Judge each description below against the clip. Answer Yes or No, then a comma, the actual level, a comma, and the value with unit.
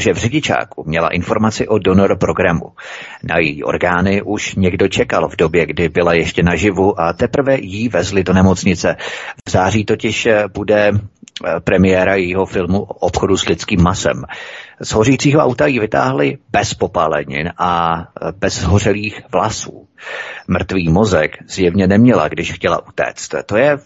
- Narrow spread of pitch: No, average, 3.6 semitones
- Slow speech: No, average, 145 wpm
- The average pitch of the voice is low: Yes, very low, 95 Hz